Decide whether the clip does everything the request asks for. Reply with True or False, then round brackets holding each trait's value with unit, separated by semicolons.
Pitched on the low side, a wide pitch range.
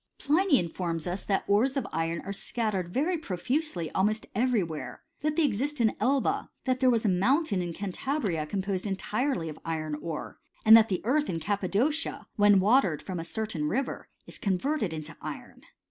False (205 Hz; 7.0 semitones)